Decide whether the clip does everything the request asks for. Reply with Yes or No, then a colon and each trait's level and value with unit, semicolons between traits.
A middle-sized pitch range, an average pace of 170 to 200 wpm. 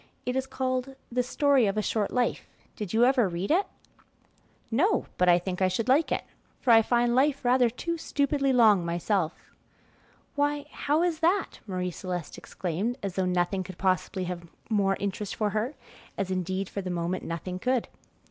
No: wide, 6.1 semitones; average, 180 wpm